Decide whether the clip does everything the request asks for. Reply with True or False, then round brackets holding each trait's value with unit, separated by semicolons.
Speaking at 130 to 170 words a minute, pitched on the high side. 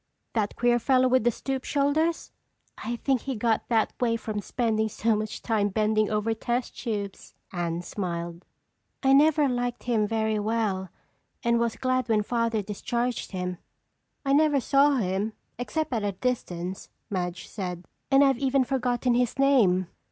True (160 wpm; 230 Hz)